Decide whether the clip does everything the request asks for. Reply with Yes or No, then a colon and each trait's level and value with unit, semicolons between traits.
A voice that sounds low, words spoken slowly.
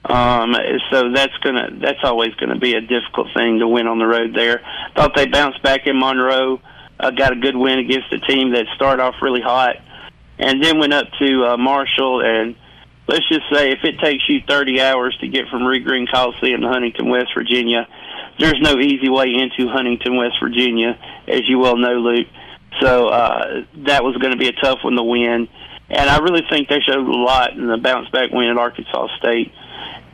No: low, 130 Hz; fast, 205 wpm